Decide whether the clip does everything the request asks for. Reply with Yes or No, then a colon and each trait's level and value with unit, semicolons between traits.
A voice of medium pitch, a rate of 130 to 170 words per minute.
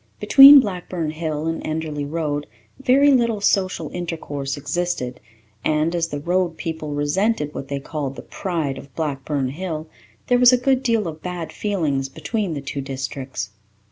Yes: medium, 160 Hz; average, 160 wpm